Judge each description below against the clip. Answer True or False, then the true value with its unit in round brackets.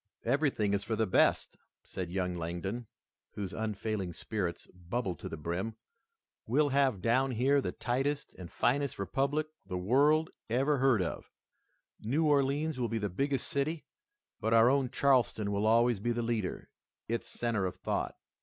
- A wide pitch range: True (5.7 semitones)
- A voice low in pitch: True (115 Hz)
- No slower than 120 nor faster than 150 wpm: False (160 wpm)